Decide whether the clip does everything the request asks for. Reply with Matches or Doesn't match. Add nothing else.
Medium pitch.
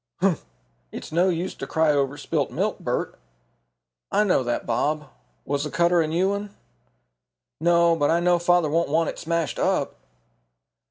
Matches